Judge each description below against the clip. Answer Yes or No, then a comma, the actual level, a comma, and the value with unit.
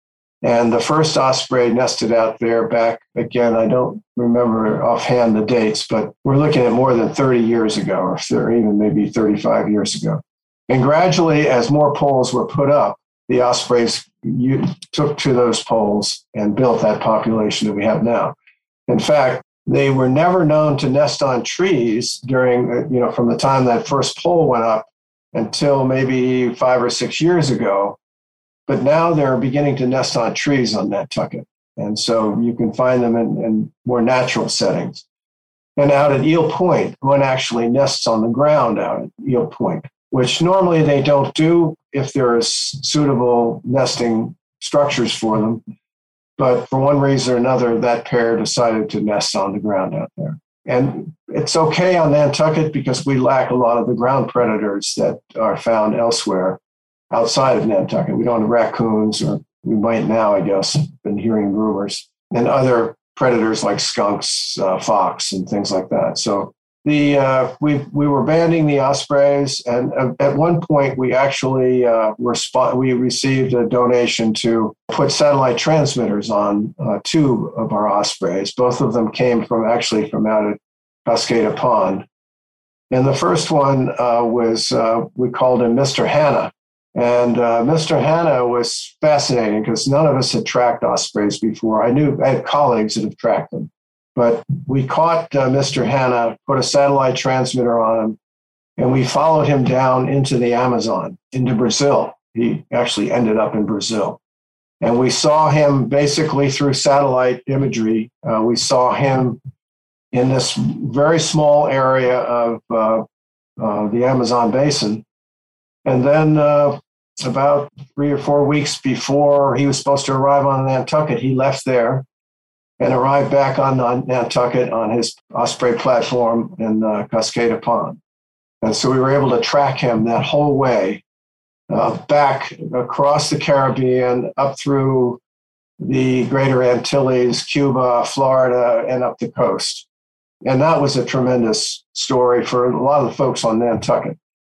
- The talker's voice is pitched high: No, low, 125 Hz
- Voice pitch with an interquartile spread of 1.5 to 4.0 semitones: Yes, average, 3.3 semitones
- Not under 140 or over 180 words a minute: Yes, average, 165 wpm